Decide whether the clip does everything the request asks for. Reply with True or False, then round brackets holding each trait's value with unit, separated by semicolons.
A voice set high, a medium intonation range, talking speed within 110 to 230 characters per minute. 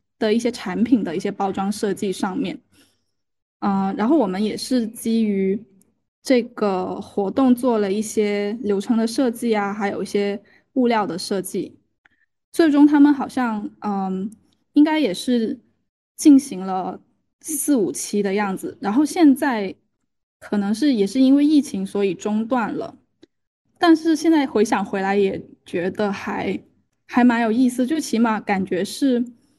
True (220 Hz; 4.8 semitones; 220 characters per minute)